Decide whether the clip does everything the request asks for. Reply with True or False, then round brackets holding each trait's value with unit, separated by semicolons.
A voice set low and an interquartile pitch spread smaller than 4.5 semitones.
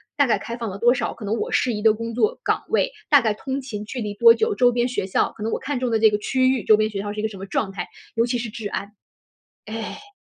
False (230 Hz; 3.3 semitones)